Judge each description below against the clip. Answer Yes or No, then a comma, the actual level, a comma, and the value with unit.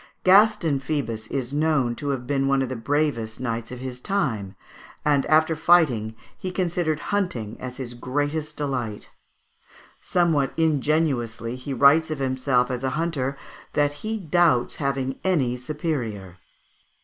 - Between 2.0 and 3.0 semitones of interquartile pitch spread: No, average, 4.1 semitones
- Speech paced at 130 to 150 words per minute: Yes, average, 140 wpm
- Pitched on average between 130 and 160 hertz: Yes, medium, 140 Hz